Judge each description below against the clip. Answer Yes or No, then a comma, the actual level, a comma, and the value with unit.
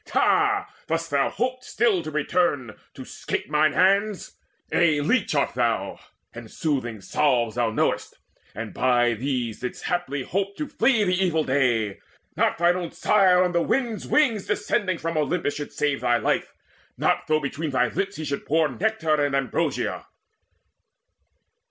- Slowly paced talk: No, average, 160 wpm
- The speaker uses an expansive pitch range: Yes, wide, 5.9 semitones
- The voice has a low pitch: No, medium, 155 Hz